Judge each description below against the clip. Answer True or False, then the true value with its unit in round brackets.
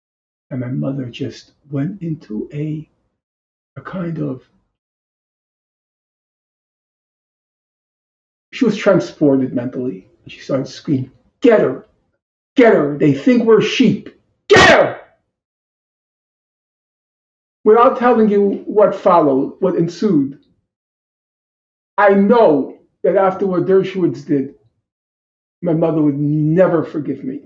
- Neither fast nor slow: False (105 wpm)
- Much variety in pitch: True (7.1 semitones)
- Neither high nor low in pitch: True (160 Hz)